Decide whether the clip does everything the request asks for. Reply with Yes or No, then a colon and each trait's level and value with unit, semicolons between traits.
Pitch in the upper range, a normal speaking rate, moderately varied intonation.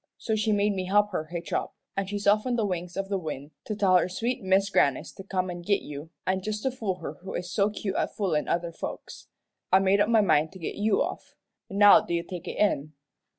No: high, 195 Hz; fast, 250 wpm; average, 3.0 semitones